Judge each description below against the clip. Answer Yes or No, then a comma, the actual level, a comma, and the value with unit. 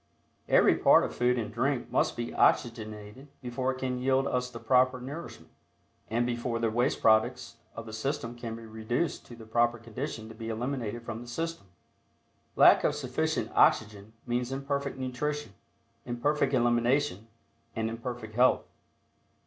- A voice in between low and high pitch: No, low, 120 Hz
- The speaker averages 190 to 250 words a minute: No, average, 155 wpm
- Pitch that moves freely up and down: No, narrow, 2.4 semitones